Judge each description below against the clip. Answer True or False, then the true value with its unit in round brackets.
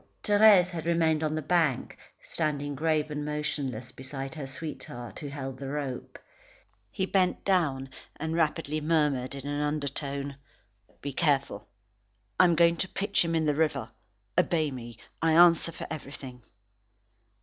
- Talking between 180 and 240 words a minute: False (150 wpm)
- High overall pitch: False (150 Hz)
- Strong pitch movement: False (3.0 semitones)